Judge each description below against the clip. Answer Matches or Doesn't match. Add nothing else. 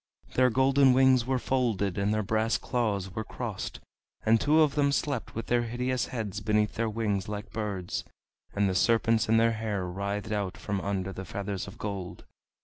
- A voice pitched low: Matches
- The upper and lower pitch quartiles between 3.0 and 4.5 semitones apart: Matches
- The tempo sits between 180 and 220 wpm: Matches